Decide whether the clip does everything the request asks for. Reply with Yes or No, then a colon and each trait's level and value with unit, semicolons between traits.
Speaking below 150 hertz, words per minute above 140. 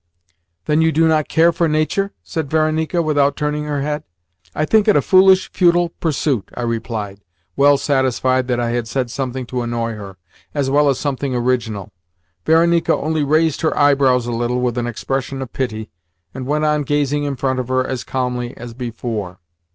Yes: low, 135 Hz; average, 185 wpm